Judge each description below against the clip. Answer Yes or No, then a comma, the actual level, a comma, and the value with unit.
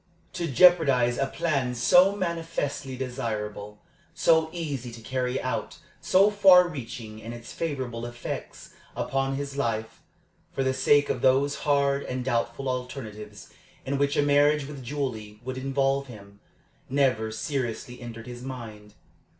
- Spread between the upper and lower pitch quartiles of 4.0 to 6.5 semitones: No, average, 3.3 semitones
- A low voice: Yes, low, 130 Hz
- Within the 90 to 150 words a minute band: Yes, average, 140 wpm